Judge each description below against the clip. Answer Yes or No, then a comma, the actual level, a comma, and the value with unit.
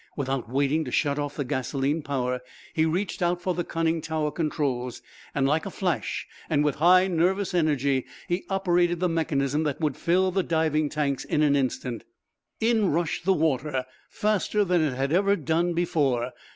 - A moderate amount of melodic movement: Yes, average, 4.0 semitones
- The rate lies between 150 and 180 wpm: Yes, average, 175 wpm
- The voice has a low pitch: No, medium, 155 Hz